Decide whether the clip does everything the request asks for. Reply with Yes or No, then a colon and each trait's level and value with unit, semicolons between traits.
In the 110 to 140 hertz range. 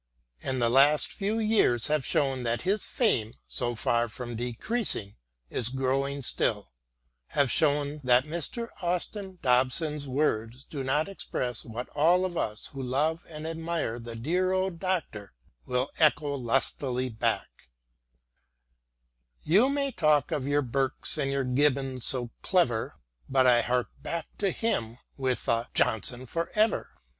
Yes: low, 135 Hz